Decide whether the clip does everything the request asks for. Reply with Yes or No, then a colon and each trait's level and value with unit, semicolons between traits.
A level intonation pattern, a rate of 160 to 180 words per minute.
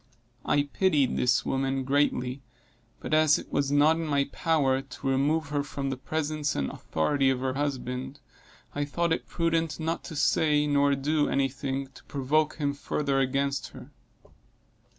Yes: narrow, 2.1 semitones; average, 165 wpm